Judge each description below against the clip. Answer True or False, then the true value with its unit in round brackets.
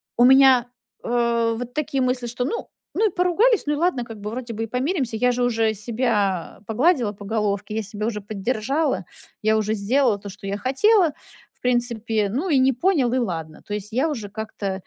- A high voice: True (235 Hz)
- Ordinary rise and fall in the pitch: True (3.8 semitones)